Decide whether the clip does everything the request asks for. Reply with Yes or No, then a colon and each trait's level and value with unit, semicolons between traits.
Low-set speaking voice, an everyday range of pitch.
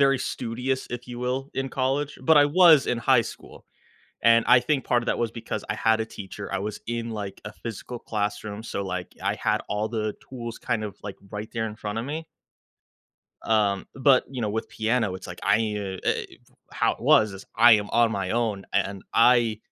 Yes: low, 115 Hz; average, 3.2 semitones